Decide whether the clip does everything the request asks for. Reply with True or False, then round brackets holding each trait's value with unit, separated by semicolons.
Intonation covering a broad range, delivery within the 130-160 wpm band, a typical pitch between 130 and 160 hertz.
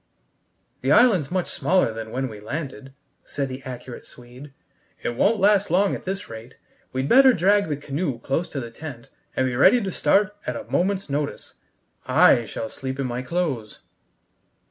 False (6.8 semitones; 175 wpm; 140 Hz)